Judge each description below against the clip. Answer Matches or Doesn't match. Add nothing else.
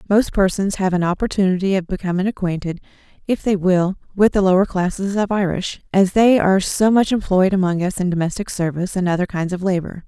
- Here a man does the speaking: Doesn't match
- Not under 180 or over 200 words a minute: Matches